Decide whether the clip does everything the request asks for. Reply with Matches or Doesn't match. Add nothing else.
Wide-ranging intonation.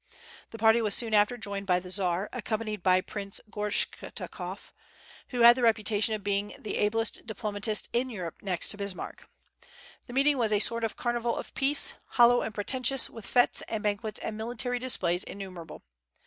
Doesn't match